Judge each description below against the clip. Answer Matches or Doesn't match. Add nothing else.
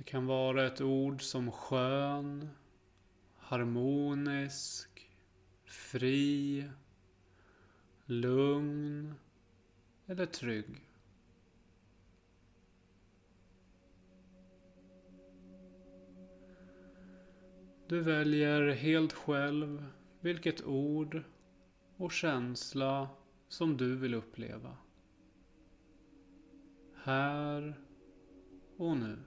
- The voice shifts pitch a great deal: Matches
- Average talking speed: Doesn't match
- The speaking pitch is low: Matches